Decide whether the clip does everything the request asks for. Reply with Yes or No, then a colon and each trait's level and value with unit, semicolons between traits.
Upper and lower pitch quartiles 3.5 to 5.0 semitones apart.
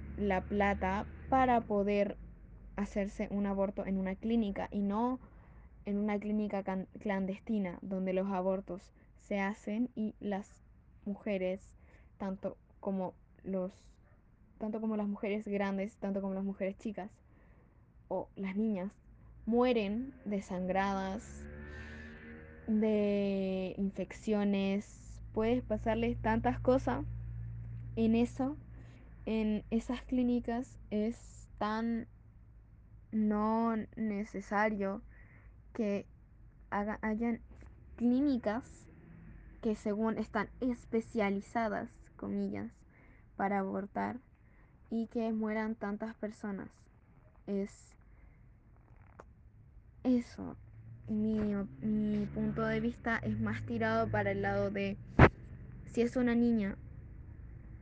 No: average, 3.1 semitones